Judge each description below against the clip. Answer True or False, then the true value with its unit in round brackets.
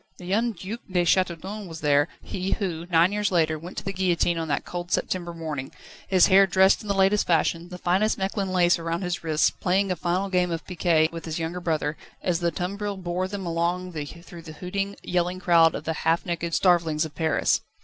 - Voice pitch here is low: False (175 Hz)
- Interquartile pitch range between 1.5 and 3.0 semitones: True (2.4 semitones)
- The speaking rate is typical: False (210 wpm)